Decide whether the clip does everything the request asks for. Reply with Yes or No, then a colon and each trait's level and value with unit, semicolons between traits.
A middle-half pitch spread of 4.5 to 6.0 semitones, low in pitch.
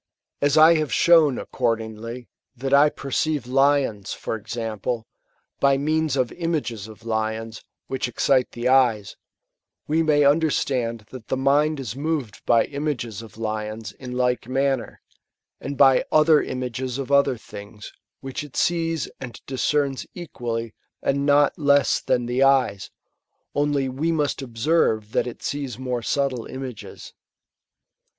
No: average, 3.8 semitones; low, 130 Hz